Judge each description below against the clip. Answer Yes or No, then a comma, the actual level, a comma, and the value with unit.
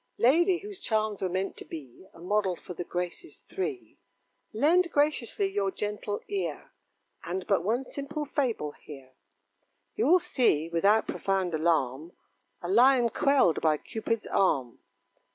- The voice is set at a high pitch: Yes, high, 210 Hz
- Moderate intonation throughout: No, wide, 8.2 semitones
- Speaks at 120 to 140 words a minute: Yes, slow, 135 wpm